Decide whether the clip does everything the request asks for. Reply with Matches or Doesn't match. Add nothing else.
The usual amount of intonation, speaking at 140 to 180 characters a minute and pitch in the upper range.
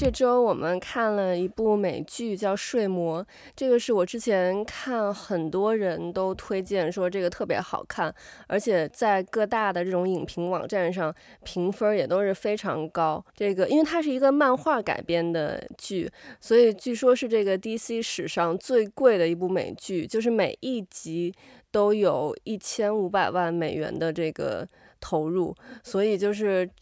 Doesn't match